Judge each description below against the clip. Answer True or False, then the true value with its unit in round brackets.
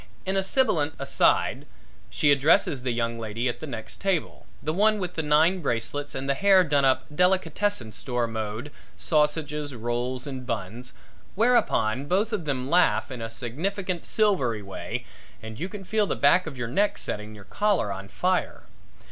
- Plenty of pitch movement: True (7.6 semitones)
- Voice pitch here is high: False (145 Hz)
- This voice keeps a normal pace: True (170 wpm)